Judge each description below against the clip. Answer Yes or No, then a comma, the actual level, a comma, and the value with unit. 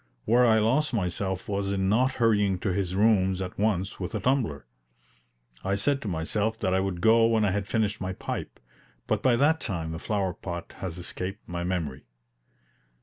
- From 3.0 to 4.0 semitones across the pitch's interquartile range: Yes, average, 3.4 semitones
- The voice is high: No, low, 100 Hz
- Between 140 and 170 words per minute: No, average, 190 wpm